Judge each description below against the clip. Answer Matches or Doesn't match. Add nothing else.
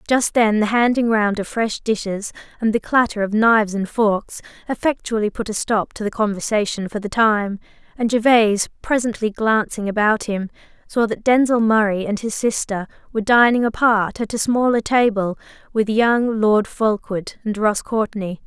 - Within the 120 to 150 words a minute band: Doesn't match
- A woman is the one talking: Matches